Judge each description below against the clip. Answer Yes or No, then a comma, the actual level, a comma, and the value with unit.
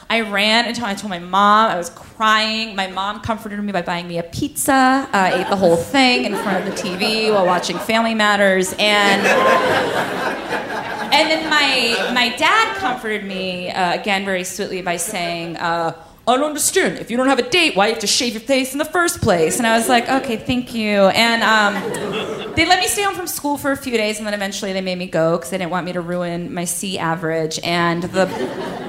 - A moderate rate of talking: No, fast, 225 wpm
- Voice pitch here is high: Yes, high, 210 Hz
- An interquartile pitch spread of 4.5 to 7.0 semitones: Yes, average, 5.2 semitones